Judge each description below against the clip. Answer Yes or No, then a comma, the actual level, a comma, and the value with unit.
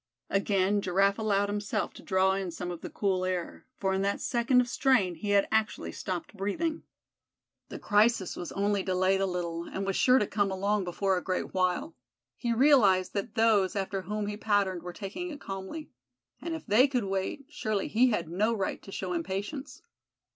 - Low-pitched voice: No, high, 200 Hz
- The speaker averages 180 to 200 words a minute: Yes, average, 190 wpm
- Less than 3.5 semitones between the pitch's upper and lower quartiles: Yes, average, 2.7 semitones